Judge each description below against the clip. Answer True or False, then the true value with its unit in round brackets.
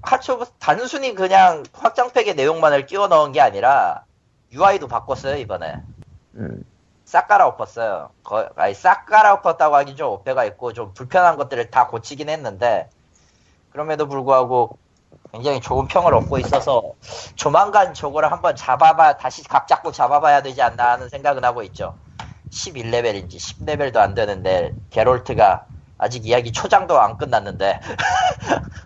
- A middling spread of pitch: False (8.0 semitones)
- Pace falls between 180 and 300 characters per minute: False (320 characters per minute)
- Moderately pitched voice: True (145 Hz)